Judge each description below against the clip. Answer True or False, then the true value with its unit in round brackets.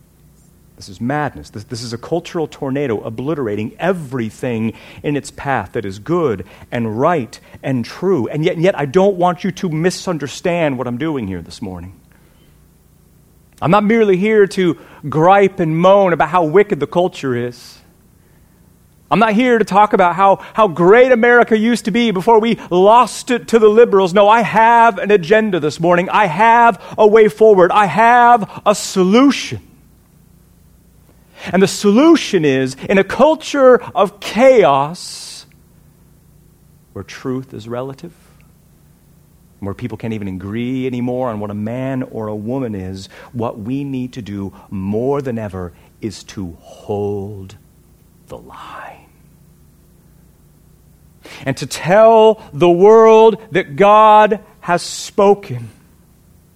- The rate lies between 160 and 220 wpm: False (145 wpm)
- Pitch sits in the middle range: True (170 Hz)